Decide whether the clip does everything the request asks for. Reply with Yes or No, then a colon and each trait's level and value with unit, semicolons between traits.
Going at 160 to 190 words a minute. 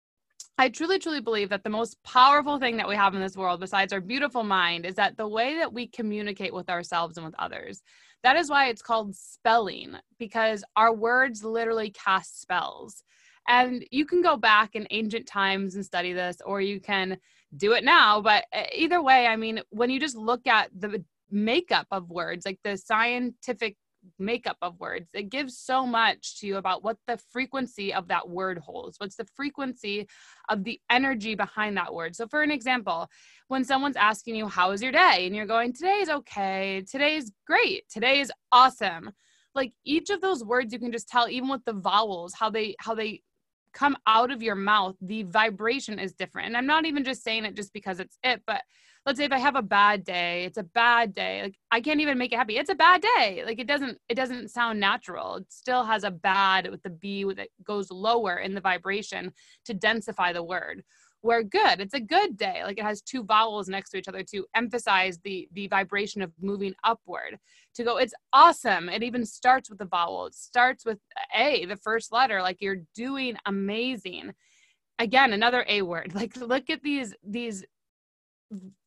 No: average, 200 wpm